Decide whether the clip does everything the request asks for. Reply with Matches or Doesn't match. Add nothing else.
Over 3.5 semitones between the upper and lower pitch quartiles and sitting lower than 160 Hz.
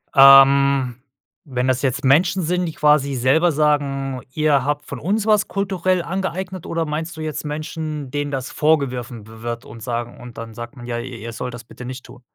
Matches